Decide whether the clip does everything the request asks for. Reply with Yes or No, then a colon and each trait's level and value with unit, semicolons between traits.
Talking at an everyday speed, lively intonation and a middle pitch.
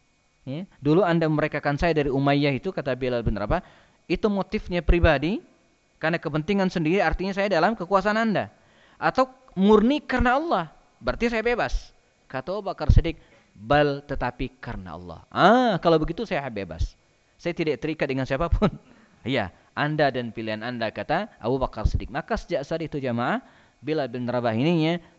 No: fast, 155 wpm; wide, 6.9 semitones; medium, 155 Hz